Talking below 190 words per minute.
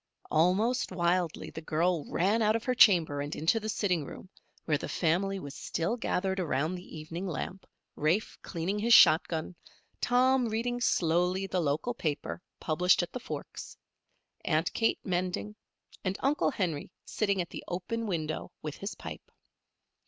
Yes: average, 160 wpm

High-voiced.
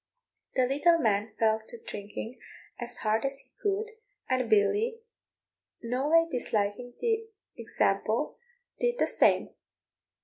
Yes: very high, 255 Hz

